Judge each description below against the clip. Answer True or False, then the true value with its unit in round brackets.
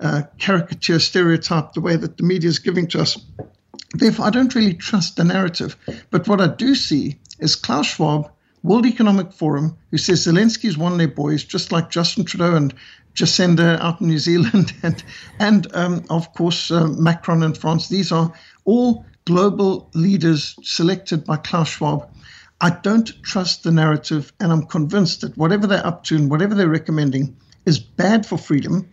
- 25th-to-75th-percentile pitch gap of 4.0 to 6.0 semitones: False (3.2 semitones)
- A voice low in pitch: False (170 Hz)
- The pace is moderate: True (180 wpm)